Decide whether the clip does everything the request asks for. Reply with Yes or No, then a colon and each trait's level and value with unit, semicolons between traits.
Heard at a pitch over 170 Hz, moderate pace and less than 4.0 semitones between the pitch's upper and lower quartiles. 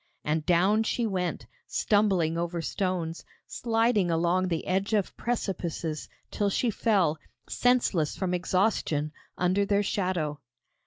No: medium, 185 Hz; slow, 120 wpm; average, 3.6 semitones